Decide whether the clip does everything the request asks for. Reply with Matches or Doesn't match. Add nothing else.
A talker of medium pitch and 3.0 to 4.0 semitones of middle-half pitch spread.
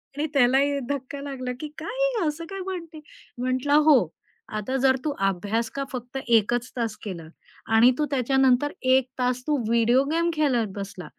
Doesn't match